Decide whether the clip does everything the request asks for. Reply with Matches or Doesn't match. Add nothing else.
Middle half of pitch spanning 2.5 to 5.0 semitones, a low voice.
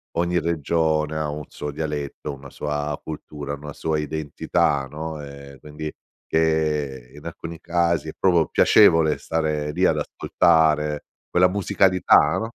Doesn't match